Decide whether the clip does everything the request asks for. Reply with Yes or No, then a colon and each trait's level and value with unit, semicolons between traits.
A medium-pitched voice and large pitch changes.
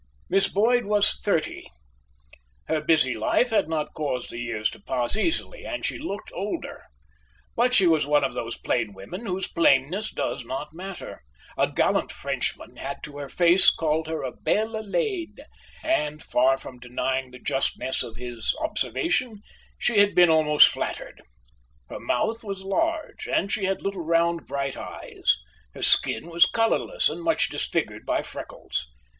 Yes: medium, 170 Hz; wide, 8.0 semitones